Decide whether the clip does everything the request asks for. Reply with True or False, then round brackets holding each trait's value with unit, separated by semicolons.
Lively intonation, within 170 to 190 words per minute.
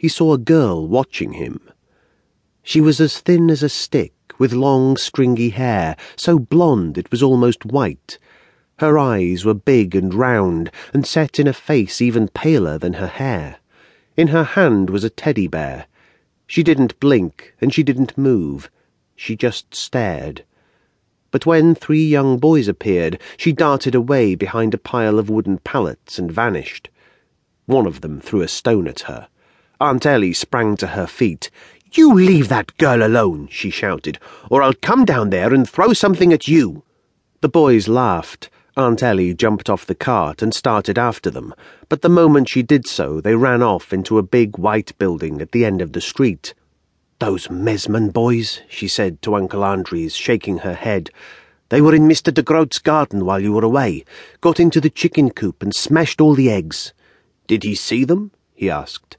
True (7.0 semitones; 175 wpm)